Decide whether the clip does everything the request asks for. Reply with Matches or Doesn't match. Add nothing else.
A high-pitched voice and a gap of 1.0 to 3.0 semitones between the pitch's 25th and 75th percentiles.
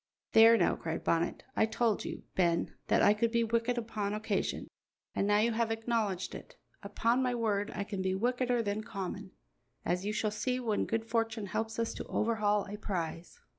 Matches